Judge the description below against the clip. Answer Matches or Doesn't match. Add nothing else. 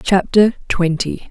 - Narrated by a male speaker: Doesn't match